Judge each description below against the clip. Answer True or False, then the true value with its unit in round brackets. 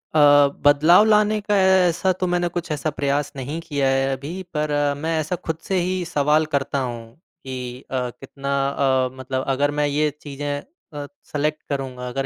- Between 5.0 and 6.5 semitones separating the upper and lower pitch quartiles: False (3.8 semitones)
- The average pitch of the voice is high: False (145 Hz)